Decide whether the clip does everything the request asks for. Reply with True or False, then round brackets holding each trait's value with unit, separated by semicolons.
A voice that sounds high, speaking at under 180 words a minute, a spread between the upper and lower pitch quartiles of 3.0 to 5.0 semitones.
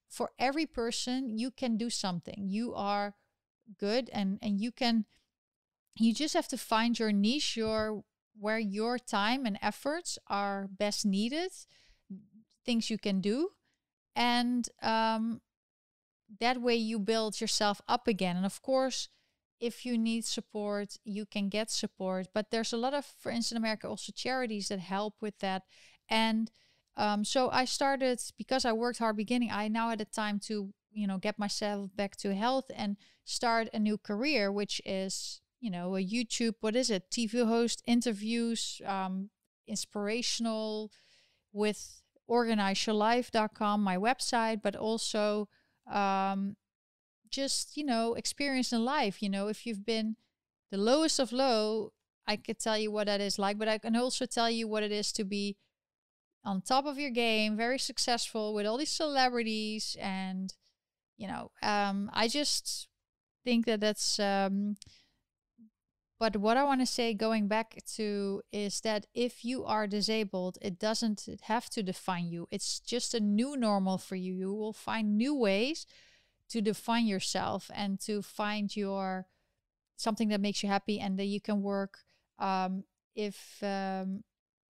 False (215 Hz; 160 wpm; 2.6 semitones)